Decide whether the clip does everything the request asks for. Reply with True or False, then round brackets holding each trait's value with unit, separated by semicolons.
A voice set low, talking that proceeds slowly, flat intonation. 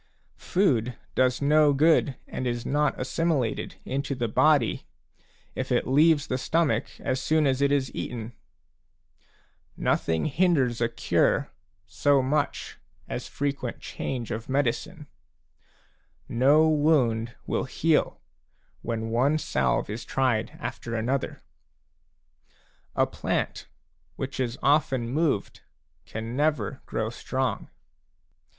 False (130 Hz; 115 wpm; 3.9 semitones)